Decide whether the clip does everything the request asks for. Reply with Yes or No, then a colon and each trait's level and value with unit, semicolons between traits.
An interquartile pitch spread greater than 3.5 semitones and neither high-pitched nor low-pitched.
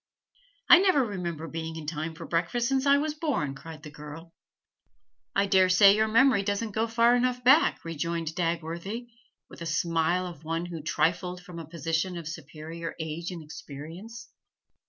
Yes: average, 5.1 semitones; medium, 170 Hz